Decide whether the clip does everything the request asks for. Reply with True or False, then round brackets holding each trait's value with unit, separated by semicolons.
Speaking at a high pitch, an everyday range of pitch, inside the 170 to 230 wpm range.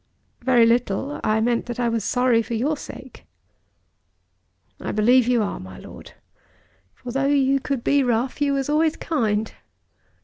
False (245 Hz; 3.2 semitones; 160 wpm)